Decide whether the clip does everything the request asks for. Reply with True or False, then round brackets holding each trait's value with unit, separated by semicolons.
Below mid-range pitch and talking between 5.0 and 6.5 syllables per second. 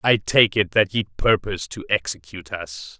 True (95 Hz; 5.2 syllables/s)